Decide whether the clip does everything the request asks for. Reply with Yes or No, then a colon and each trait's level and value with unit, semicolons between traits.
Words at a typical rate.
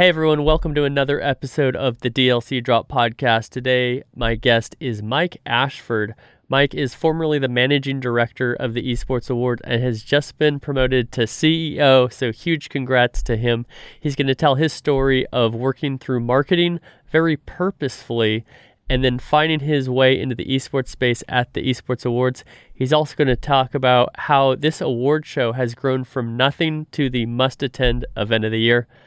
Yes: average, 180 wpm